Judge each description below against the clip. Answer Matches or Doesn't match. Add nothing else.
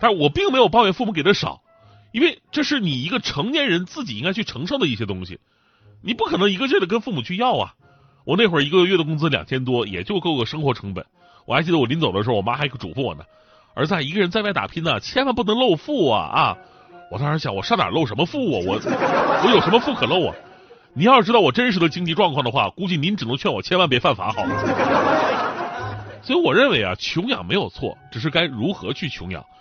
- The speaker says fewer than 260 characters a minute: Doesn't match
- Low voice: Doesn't match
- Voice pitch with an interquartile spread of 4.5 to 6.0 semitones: Doesn't match